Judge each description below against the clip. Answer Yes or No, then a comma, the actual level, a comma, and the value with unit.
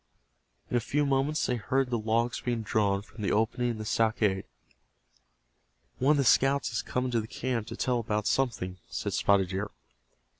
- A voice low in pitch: Yes, low, 115 Hz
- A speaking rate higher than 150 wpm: Yes, average, 185 wpm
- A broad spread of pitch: No, average, 3.2 semitones